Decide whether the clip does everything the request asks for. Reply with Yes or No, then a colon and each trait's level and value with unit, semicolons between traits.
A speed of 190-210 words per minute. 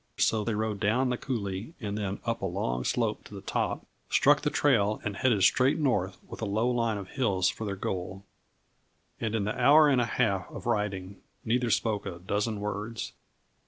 Yes: average, 195 wpm